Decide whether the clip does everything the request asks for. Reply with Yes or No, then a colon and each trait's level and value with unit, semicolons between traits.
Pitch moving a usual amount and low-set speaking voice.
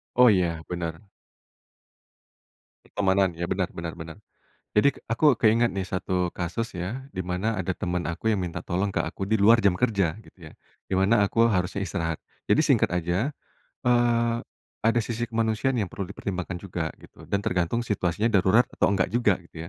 Yes: average, 4.3 semitones; very low, 95 Hz